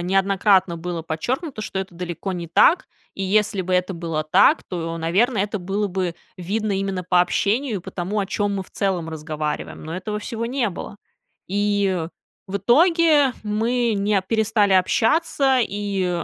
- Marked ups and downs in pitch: No, average, 3.4 semitones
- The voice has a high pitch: Yes, high, 195 Hz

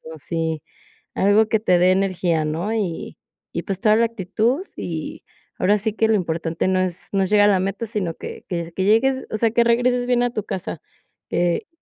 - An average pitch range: Yes, average, 4.1 semitones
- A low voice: No, high, 195 Hz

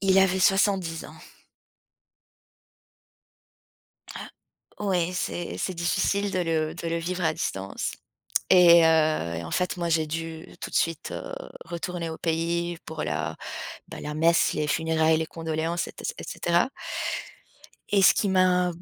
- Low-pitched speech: No, medium, 170 Hz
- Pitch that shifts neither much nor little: No, narrow, 2.0 semitones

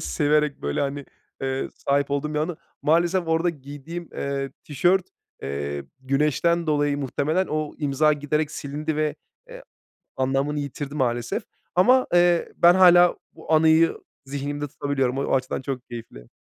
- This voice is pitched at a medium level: Yes, medium, 145 Hz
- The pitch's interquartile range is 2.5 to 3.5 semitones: Yes, average, 3.0 semitones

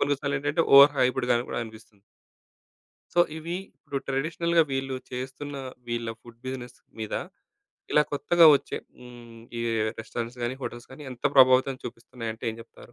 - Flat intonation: No, average, 3.1 semitones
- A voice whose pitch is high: No, low, 130 Hz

